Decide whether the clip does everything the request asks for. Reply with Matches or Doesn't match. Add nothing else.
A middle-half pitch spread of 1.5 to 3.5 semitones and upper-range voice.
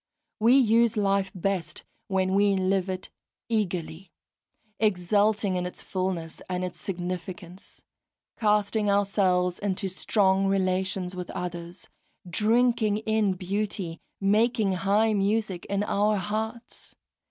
Matches